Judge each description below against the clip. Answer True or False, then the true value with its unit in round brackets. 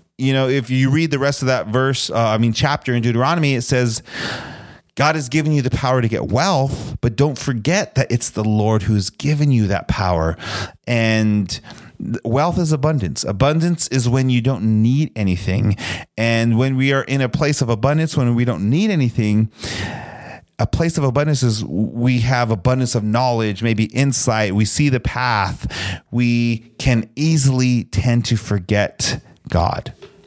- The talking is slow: False (170 wpm)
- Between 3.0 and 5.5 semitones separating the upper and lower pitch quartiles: True (3.7 semitones)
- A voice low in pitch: True (125 Hz)